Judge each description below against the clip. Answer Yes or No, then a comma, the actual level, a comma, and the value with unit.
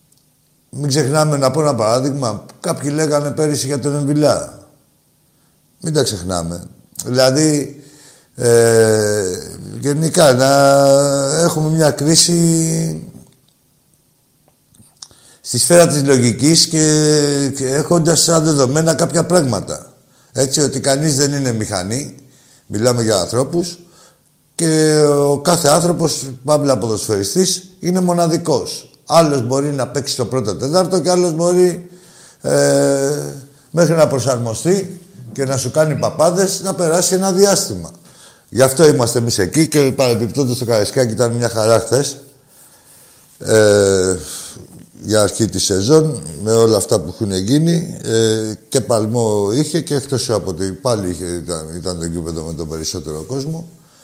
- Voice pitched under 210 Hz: Yes, medium, 140 Hz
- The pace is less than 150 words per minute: Yes, average, 130 wpm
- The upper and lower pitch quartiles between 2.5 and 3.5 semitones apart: No, average, 5.1 semitones